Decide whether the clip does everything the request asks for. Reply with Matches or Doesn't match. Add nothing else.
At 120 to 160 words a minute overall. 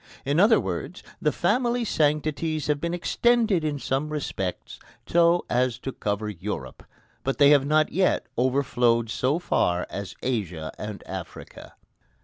Matches